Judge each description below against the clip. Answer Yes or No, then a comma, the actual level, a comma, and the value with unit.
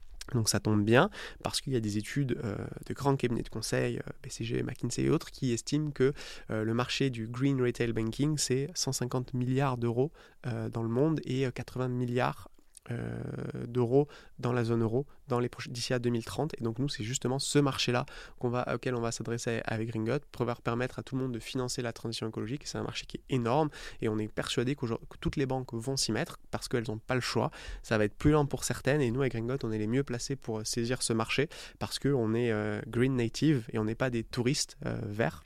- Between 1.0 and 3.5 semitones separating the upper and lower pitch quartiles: Yes, average, 2.9 semitones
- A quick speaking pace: Yes, fast, 230 wpm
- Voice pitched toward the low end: Yes, low, 125 Hz